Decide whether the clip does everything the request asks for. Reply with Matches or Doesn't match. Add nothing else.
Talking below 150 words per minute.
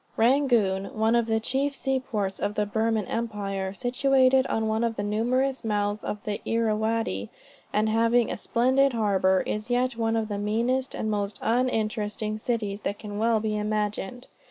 Doesn't match